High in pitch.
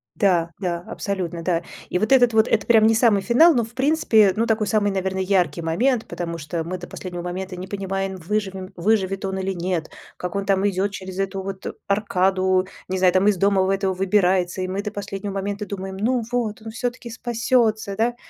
Yes: high, 195 Hz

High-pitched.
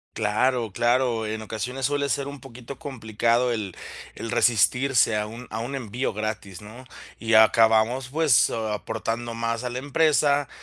No: low, 120 Hz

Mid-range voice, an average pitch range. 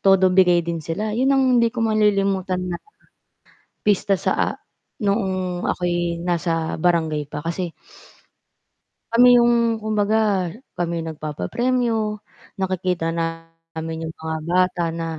Yes: medium, 180 Hz; average, 4.3 semitones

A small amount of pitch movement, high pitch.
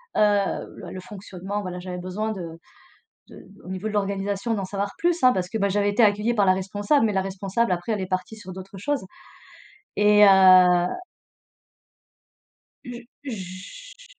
Yes: narrow, 2.3 semitones; high, 200 Hz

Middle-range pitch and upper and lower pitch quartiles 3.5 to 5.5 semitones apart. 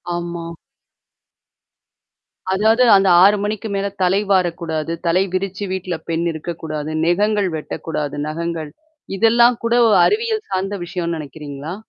Yes: medium, 180 Hz; average, 3.8 semitones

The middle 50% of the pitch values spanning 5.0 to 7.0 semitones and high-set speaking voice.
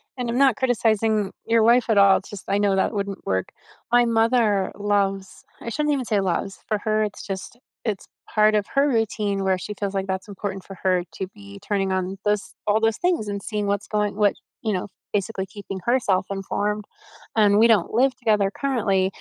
No: narrow, 2.5 semitones; high, 205 Hz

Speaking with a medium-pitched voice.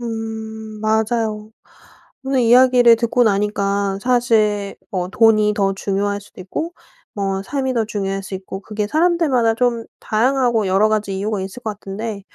No: high, 215 Hz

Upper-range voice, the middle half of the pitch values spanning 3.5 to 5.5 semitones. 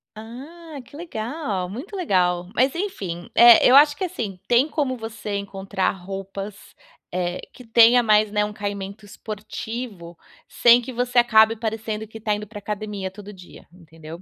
Yes: high, 215 Hz; average, 3.8 semitones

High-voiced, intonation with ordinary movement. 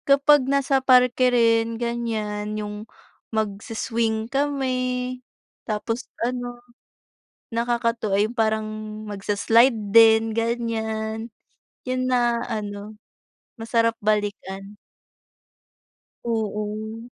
No: high, 225 Hz; narrow, 2.0 semitones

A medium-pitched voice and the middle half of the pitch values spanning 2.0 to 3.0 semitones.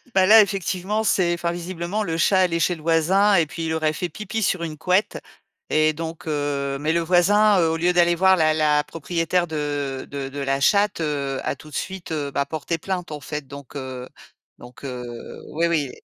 No: medium, 165 Hz; average, 3.6 semitones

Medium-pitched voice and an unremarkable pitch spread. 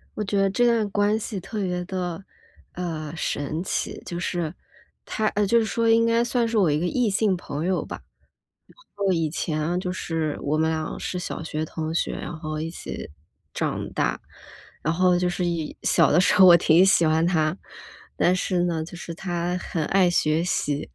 Yes: medium, 175 Hz; average, 3.4 semitones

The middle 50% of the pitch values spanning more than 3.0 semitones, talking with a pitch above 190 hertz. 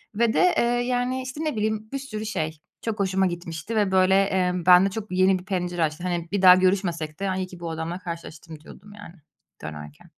No: average, 3.7 semitones; medium, 185 Hz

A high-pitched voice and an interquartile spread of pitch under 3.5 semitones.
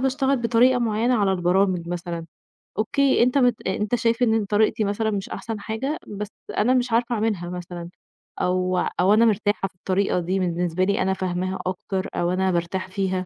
No: high, 200 Hz; average, 3.8 semitones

